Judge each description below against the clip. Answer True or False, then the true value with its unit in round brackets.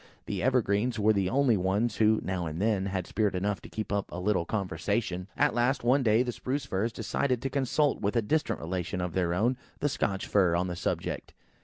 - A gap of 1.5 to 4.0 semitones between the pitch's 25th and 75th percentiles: False (4.5 semitones)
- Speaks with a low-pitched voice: True (105 Hz)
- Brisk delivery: True (215 wpm)